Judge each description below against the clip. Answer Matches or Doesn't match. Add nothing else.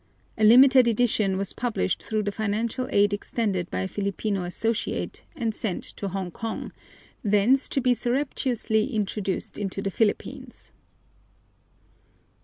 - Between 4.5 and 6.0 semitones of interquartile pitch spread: Doesn't match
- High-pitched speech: Matches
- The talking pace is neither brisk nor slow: Doesn't match